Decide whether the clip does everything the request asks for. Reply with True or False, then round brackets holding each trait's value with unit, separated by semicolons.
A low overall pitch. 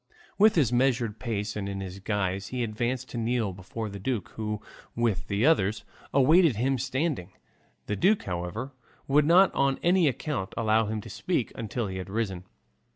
True (115 Hz)